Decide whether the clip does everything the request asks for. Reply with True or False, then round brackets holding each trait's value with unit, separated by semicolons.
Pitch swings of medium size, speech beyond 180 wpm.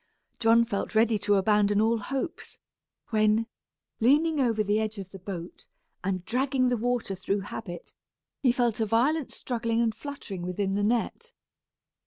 False (3.2 semitones; 155 wpm)